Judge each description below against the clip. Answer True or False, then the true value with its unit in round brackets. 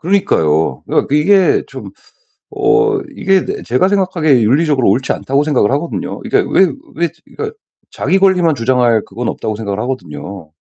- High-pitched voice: False (145 Hz)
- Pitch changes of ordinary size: False (8.8 semitones)